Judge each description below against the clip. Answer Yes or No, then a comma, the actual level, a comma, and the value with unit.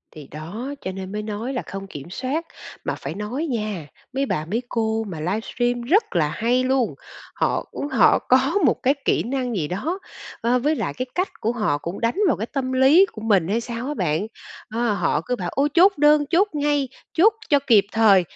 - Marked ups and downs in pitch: Yes, wide, 5.8 semitones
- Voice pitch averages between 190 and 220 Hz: No, high, 235 Hz